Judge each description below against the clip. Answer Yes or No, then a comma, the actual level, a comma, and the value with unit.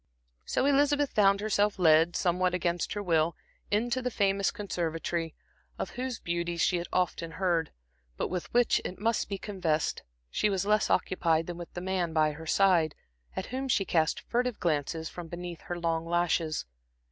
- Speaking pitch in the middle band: Yes, medium, 180 Hz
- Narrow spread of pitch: No, average, 3.7 semitones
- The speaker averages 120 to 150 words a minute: No, average, 170 wpm